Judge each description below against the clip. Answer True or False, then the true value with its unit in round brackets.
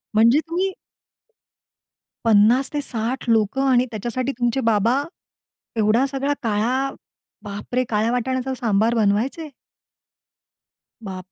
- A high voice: True (235 Hz)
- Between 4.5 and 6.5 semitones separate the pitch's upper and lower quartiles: False (3.5 semitones)